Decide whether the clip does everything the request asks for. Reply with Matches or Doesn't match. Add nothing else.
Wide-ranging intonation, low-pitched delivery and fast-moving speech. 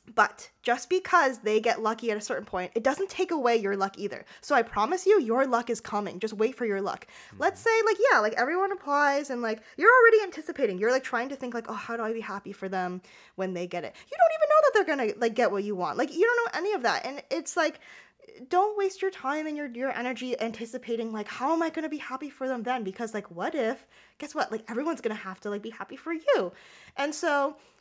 Doesn't match